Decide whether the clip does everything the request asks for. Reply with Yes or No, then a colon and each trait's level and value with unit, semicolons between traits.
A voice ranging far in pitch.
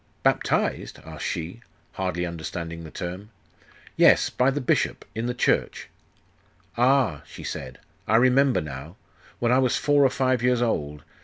Yes: wide, 7.4 semitones